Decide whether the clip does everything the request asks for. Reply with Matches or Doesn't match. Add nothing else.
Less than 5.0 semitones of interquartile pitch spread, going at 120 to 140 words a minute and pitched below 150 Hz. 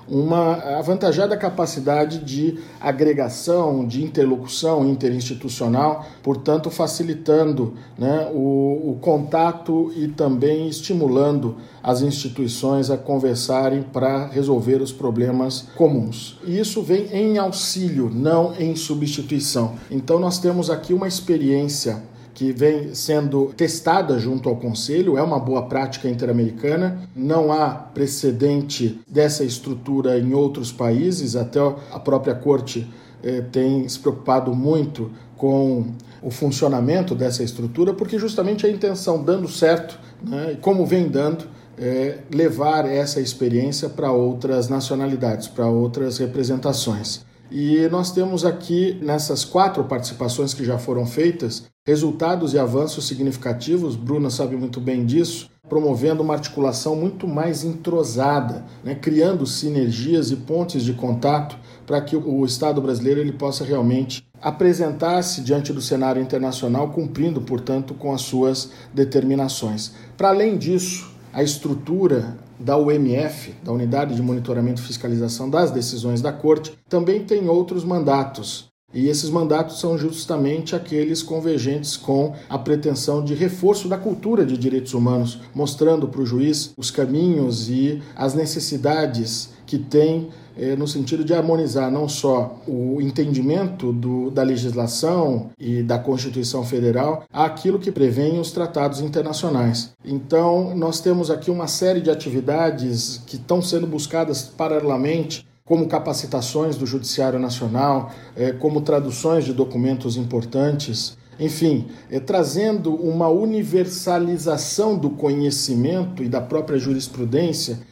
Matches